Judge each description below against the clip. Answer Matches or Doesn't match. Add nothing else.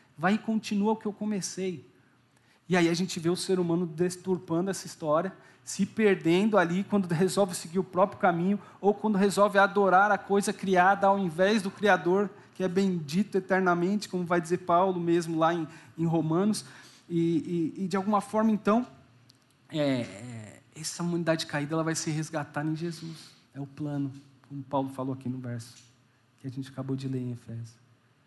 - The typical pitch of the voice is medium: Matches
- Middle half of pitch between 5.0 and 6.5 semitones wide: Matches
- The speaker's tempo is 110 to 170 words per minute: Doesn't match